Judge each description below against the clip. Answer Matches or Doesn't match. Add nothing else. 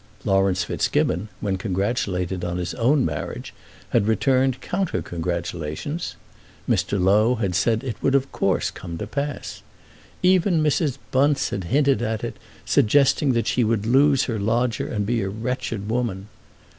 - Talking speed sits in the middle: Matches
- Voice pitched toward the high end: Doesn't match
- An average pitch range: Doesn't match